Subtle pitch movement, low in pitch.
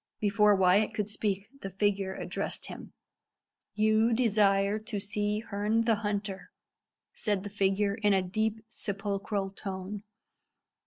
No: narrow, 1.6 semitones; high, 205 Hz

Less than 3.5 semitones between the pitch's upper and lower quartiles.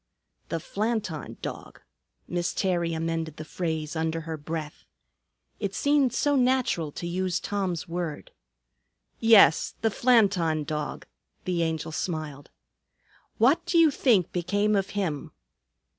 No: average, 4.7 semitones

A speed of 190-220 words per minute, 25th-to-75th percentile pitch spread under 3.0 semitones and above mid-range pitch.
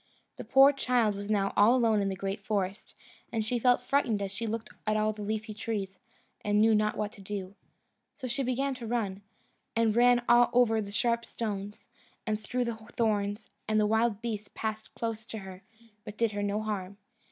Yes: average, 195 wpm; narrow, 2.4 semitones; high, 215 Hz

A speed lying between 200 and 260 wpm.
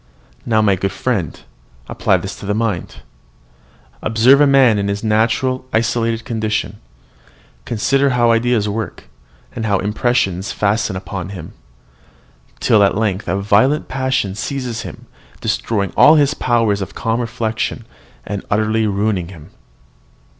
No: slow, 135 wpm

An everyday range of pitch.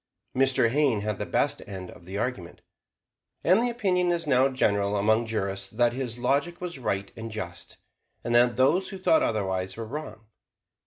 No: wide, 5.8 semitones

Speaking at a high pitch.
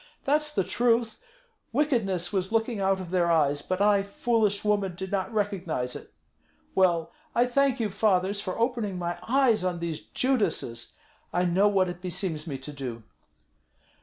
Yes: high, 195 Hz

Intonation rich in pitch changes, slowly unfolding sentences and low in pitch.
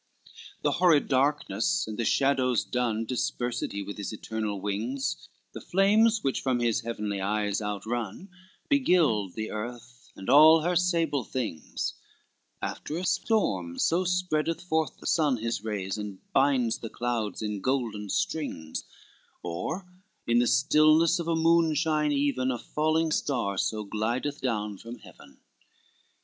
No: wide, 6.6 semitones; average, 145 wpm; low, 125 Hz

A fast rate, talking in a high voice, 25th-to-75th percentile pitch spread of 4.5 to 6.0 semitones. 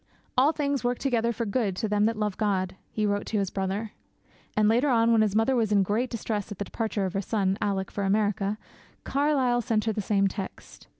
No: fast, 225 wpm; high, 215 Hz; narrow, 2.6 semitones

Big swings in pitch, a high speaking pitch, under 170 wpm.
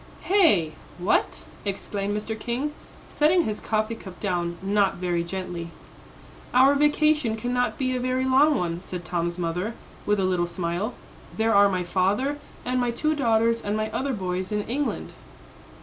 Yes: wide, 5.7 semitones; high, 215 Hz; average, 160 wpm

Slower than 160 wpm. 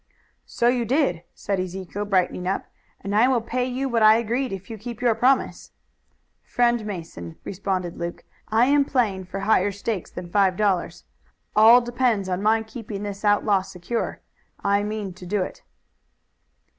No: average, 165 wpm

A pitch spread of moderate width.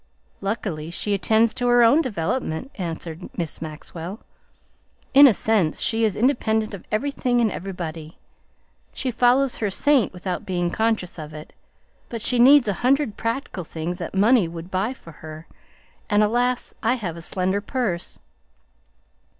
No: wide, 5.9 semitones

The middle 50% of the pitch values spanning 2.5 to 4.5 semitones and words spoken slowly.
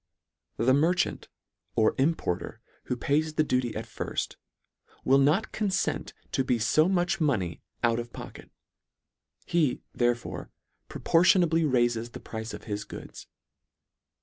No: wide, 5.4 semitones; slow, 130 wpm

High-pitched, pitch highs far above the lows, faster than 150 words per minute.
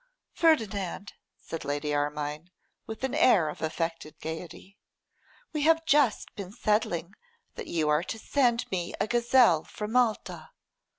No: high, 200 Hz; wide, 7.1 semitones; slow, 135 wpm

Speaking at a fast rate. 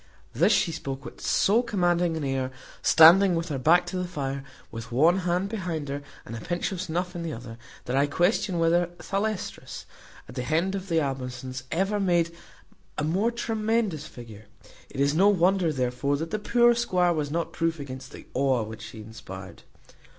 No: average, 185 wpm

